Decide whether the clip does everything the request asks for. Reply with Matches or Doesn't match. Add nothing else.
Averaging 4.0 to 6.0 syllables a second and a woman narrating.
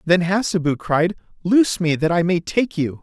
Doesn't match